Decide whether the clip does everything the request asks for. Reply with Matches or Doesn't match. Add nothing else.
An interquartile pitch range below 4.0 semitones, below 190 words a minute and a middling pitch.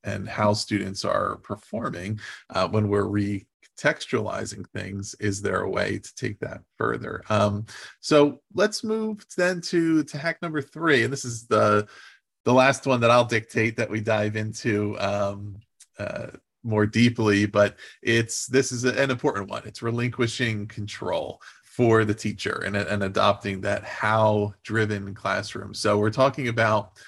Doesn't match